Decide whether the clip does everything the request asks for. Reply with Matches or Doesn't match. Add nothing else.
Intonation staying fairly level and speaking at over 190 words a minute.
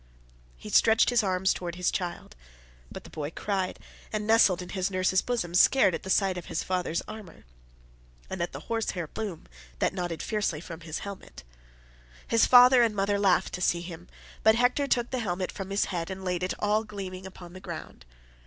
Doesn't match